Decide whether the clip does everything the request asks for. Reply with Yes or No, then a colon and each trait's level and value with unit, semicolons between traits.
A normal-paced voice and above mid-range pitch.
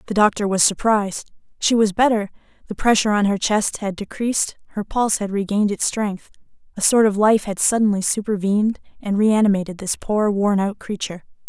Yes: average, 180 wpm; high, 205 Hz